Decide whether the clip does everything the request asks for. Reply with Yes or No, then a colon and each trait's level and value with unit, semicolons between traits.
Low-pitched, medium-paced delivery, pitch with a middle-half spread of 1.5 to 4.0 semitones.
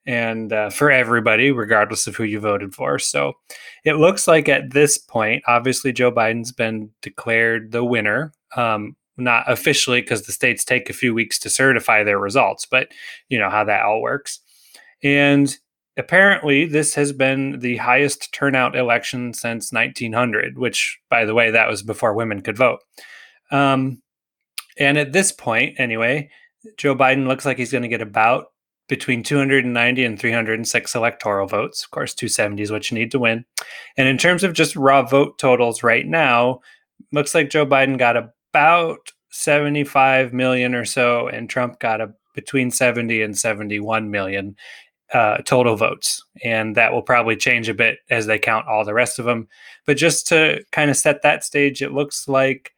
Yes: low, 125 Hz; average, 175 wpm; average, 3.6 semitones